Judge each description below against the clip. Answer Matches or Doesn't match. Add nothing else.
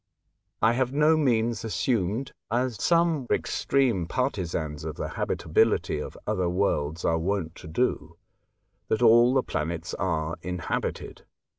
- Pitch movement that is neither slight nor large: Doesn't match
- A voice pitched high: Doesn't match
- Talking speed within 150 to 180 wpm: Doesn't match